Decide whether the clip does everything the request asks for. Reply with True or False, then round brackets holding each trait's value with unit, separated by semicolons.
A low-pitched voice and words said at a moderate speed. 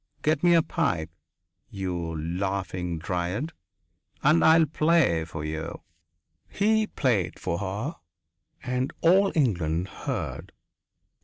False (100 Hz; 110 wpm)